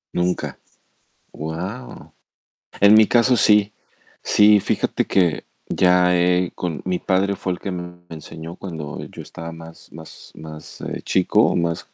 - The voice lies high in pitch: No, very low, 90 Hz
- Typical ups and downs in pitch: Yes, average, 3.2 semitones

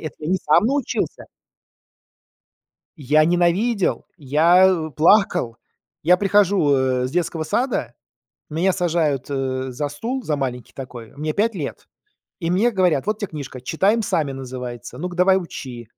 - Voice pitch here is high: No, medium, 160 Hz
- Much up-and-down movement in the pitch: Yes, wide, 5.9 semitones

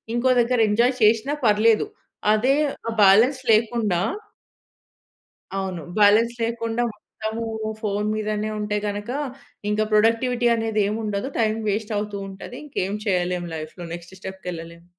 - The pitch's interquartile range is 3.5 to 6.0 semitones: No, narrow, 2.5 semitones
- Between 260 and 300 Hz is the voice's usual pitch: No, high, 215 Hz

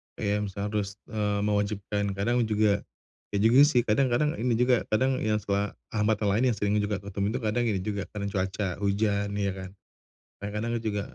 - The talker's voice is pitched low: Yes, low, 105 Hz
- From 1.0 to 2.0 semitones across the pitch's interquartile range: Yes, narrow, 1.6 semitones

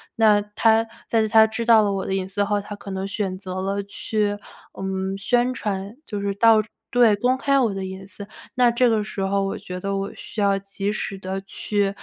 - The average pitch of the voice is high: Yes, high, 205 Hz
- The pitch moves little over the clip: Yes, narrow, 2.1 semitones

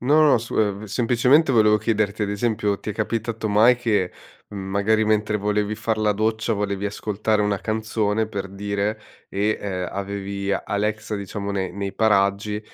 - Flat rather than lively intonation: Yes, narrow, 1.6 semitones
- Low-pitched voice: Yes, low, 105 Hz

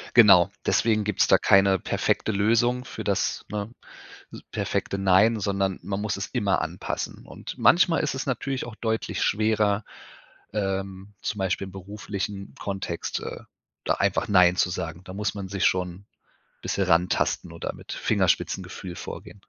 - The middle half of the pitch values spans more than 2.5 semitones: No, narrow, 2.1 semitones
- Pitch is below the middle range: Yes, low, 100 Hz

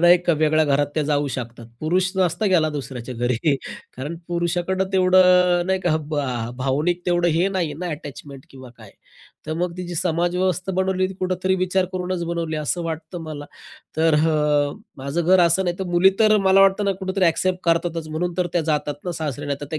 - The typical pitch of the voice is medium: Yes, medium, 170 Hz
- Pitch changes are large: No, average, 3.5 semitones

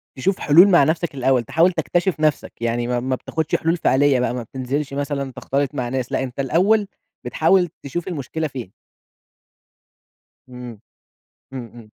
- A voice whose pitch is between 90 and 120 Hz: No, medium, 140 Hz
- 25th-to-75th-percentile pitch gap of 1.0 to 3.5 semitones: No, average, 4.4 semitones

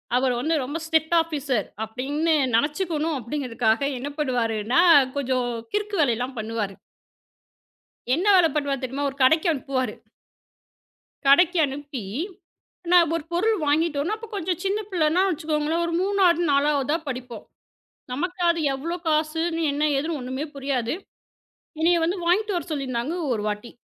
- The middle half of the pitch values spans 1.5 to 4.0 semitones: No, average, 4.7 semitones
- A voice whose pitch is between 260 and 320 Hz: Yes, very high, 295 Hz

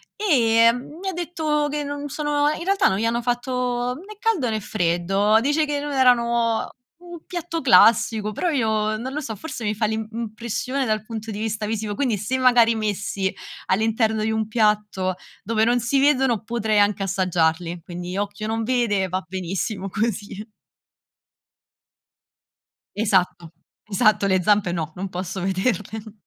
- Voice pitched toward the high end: Yes, high, 220 Hz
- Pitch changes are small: No, average, 3.9 semitones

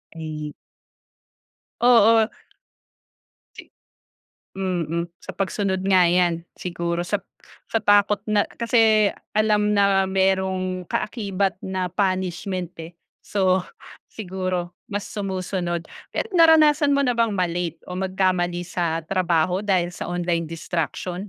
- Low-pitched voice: No, medium, 185 Hz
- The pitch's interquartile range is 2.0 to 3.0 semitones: Yes, average, 2.7 semitones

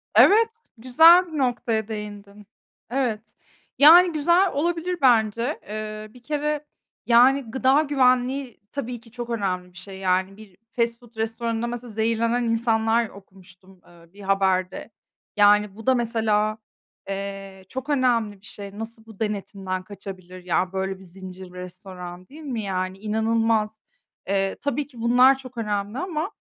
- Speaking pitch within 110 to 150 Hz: No, high, 220 Hz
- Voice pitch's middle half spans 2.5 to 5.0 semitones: Yes, average, 4.2 semitones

